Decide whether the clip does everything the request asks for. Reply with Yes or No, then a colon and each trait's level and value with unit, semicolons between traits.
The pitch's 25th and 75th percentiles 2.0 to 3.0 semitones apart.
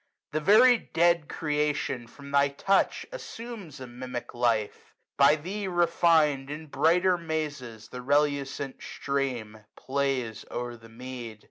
No: average, 4.7 semitones